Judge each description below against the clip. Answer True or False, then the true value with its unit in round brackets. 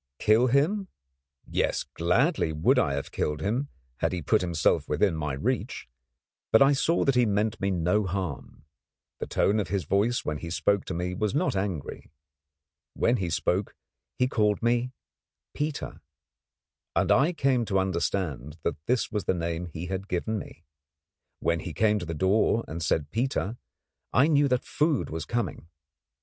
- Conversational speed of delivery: True (170 wpm)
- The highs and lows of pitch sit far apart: True (6.3 semitones)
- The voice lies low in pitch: True (100 Hz)